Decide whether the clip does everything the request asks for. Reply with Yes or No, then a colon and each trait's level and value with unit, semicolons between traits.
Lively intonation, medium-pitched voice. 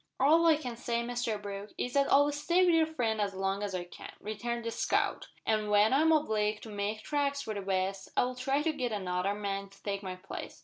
No: wide, 5.7 semitones; high, 220 Hz